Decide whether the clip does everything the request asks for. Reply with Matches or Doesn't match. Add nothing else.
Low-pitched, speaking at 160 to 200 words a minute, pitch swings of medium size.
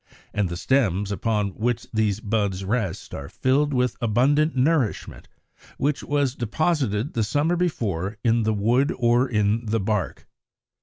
Doesn't match